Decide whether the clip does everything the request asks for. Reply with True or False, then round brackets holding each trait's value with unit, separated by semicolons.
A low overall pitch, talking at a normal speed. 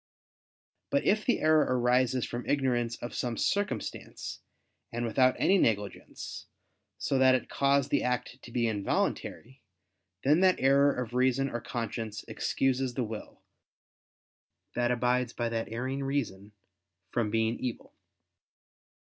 False (125 Hz; 130 wpm)